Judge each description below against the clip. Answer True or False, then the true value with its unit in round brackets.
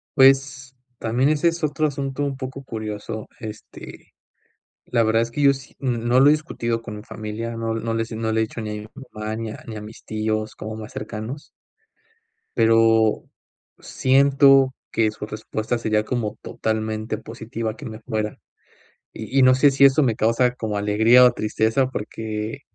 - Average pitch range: True (3.3 semitones)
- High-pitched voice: False (115 Hz)